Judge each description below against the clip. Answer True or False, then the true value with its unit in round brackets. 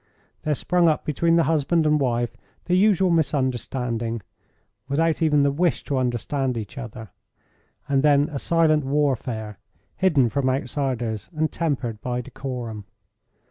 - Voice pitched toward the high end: False (140 Hz)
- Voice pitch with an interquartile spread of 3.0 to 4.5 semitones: True (4.2 semitones)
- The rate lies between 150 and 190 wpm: False (140 wpm)